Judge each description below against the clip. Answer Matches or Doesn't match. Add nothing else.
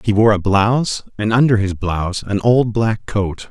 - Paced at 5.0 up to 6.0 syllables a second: Doesn't match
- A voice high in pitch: Doesn't match